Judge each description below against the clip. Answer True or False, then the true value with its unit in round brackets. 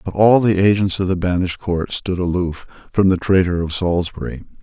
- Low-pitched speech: True (90 Hz)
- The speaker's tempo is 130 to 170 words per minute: False (195 wpm)